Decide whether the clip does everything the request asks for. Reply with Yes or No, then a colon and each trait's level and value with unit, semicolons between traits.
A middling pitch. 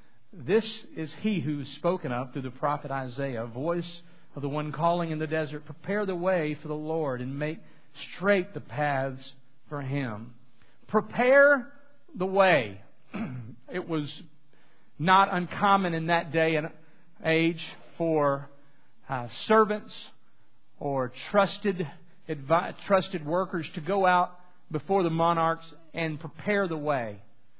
Yes: medium, 160 Hz